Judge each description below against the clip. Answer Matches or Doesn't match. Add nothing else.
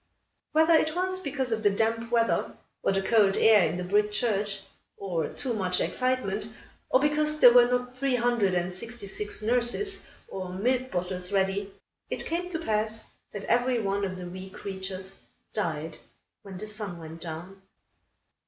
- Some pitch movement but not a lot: Matches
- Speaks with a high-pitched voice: Matches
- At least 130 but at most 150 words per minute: Doesn't match